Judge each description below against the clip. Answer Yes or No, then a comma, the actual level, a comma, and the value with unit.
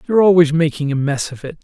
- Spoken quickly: Yes, fast, 260 wpm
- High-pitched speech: No, medium, 160 Hz